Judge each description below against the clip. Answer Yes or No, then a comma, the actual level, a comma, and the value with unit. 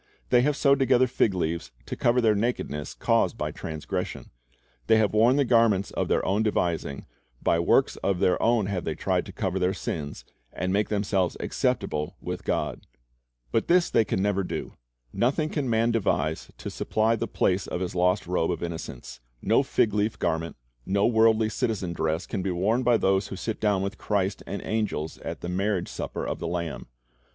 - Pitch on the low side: Yes, low, 100 Hz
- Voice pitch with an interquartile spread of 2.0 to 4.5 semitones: Yes, average, 4.1 semitones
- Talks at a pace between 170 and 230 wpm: Yes, average, 190 wpm